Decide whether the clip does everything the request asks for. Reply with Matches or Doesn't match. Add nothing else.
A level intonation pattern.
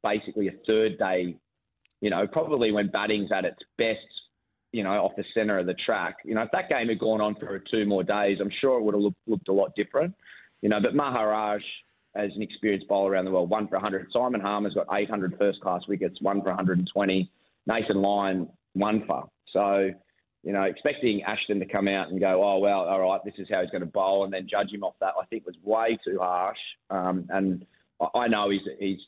Matches